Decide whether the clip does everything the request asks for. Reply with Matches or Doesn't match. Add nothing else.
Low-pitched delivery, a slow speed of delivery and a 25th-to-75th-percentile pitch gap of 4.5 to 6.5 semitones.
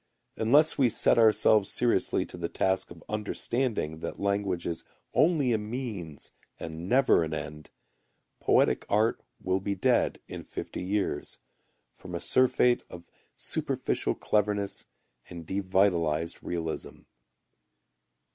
Matches